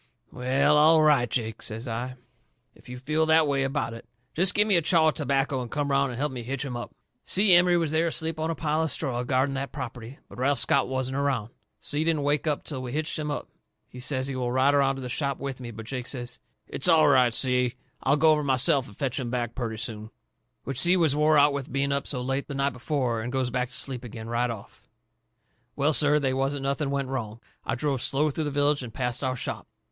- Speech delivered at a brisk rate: Yes, fast, 245 wpm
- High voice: No, low, 135 Hz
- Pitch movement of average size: Yes, average, 3.0 semitones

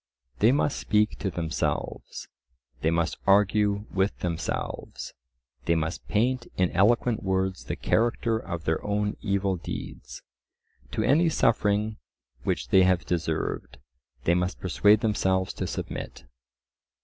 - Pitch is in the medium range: No, low, 100 Hz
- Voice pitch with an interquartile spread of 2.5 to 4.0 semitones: Yes, average, 3.3 semitones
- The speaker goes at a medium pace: No, slow, 125 wpm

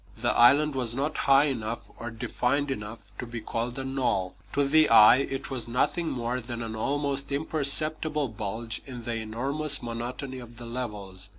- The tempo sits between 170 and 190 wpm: Yes, average, 175 wpm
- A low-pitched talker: Yes, low, 125 Hz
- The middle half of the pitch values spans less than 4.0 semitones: Yes, average, 3.3 semitones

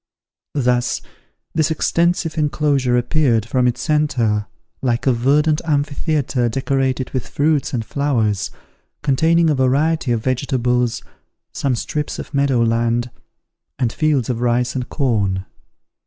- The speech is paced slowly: Yes, slow, 125 wpm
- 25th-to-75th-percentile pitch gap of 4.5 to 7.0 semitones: No, average, 3.7 semitones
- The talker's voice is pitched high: No, low, 130 Hz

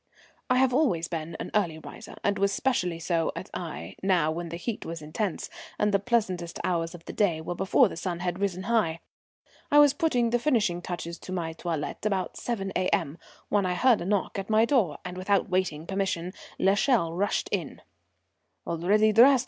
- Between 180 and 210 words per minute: Yes, average, 190 wpm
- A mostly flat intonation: No, average, 4.0 semitones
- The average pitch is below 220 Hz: Yes, medium, 185 Hz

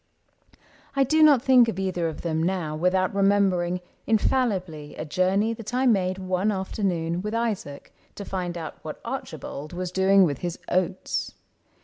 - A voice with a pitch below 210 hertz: Yes, medium, 185 Hz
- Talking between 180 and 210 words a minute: No, average, 155 wpm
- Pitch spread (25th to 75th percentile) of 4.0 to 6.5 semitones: No, average, 3.3 semitones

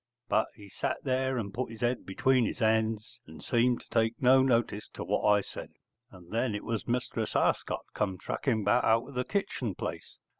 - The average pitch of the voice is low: Yes, low, 115 Hz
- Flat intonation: No, average, 3.2 semitones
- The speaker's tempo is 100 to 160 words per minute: No, average, 200 wpm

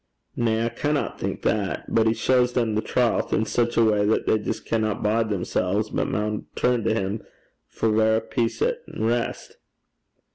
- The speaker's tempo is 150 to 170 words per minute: No, average, 180 wpm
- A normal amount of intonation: No, narrow, 1.6 semitones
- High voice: No, low, 110 Hz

